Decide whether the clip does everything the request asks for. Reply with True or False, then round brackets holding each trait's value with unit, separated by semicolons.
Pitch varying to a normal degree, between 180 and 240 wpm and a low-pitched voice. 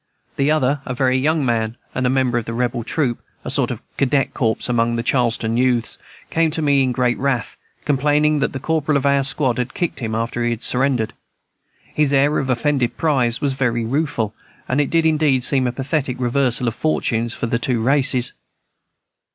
True (3.0 semitones; 200 wpm; 130 Hz)